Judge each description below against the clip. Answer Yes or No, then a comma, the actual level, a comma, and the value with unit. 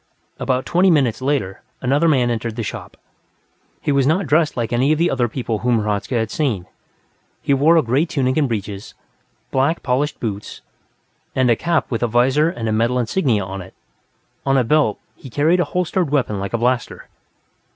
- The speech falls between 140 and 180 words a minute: No, average, 190 wpm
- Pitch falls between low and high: No, low, 130 Hz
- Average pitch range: Yes, average, 4.5 semitones